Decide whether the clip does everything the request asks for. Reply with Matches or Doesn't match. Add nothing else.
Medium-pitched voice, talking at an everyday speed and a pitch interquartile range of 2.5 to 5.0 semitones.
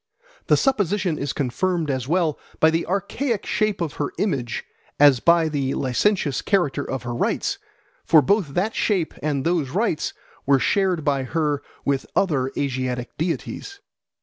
Doesn't match